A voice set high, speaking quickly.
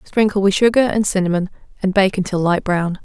No: high, 195 Hz; average, 195 wpm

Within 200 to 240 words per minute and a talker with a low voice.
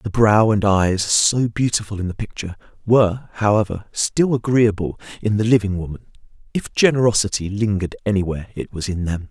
No: average, 160 wpm; low, 105 Hz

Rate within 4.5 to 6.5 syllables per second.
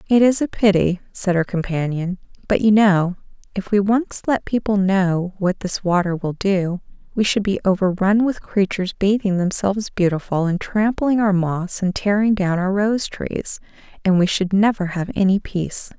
Yes: 4.7 syllables/s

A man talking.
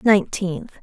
No: female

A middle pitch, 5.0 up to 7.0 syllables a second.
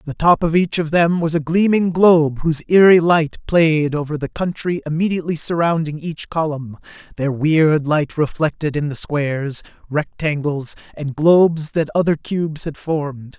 No: medium, 155 Hz; 4.8 syllables/s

